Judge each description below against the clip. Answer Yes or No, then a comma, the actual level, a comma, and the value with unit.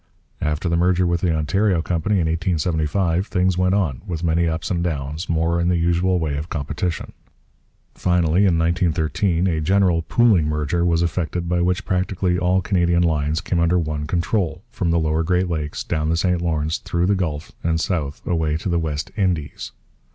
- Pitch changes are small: Yes, narrow, 2.2 semitones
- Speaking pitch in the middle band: No, very low, 85 Hz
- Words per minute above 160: Yes, average, 185 wpm